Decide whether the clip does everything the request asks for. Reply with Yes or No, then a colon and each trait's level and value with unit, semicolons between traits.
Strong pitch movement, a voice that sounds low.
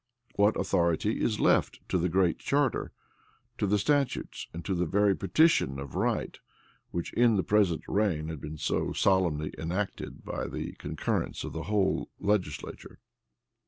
No: average, 4.0 semitones; very low, 95 Hz